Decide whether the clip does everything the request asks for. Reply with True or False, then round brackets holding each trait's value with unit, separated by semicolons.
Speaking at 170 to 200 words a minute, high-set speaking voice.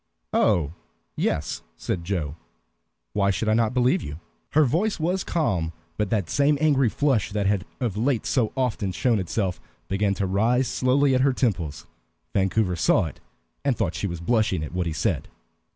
False (175 wpm; 105 Hz)